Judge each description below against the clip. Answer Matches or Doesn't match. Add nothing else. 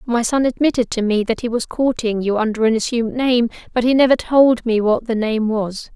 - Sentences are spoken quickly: Matches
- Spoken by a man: Doesn't match